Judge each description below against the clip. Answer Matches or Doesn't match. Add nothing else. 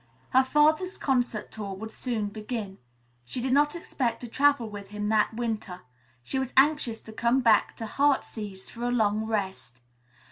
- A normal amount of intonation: Matches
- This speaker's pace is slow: Doesn't match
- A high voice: Matches